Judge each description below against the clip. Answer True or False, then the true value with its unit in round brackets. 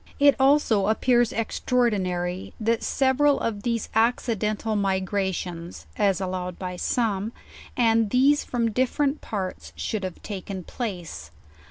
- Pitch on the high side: True (215 Hz)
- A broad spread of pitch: False (4.3 semitones)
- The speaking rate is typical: False (130 wpm)